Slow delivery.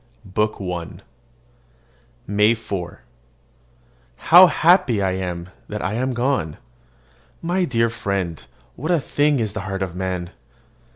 Yes: slow, 125 wpm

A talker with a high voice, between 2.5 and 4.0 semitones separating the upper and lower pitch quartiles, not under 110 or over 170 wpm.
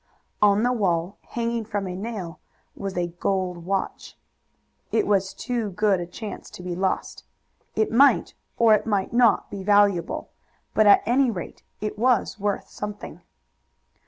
Yes: high, 205 Hz; average, 3.1 semitones; average, 155 wpm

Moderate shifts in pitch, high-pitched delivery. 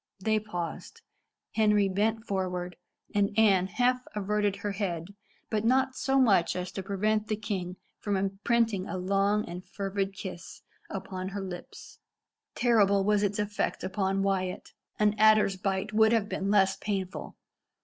No: narrow, 2.0 semitones; high, 200 Hz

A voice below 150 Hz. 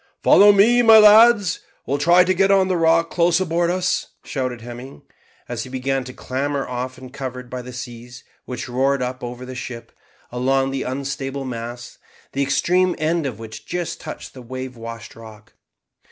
Yes: low, 135 Hz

